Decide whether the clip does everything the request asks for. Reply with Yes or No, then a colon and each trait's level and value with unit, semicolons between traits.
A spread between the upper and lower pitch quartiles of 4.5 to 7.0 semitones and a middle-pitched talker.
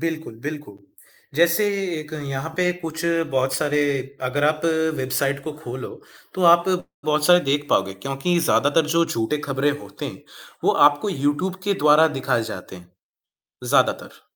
No: average, 3.3 semitones; medium, 145 Hz